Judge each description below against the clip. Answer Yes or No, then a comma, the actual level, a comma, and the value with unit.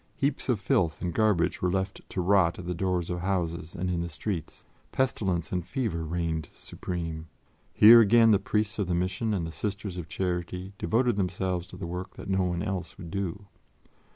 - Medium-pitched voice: No, very low, 90 Hz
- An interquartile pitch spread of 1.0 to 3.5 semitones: Yes, average, 2.8 semitones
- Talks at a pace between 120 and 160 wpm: No, average, 195 wpm